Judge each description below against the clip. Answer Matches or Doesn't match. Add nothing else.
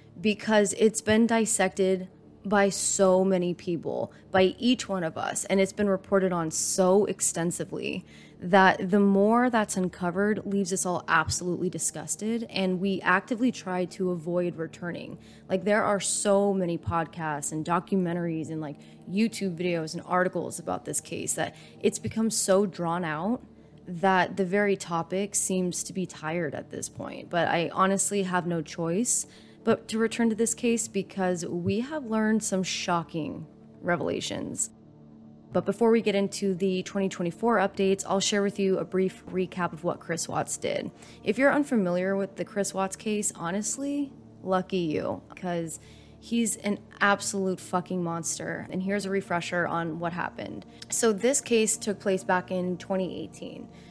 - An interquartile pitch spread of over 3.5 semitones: Doesn't match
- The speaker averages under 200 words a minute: Matches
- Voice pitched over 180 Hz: Matches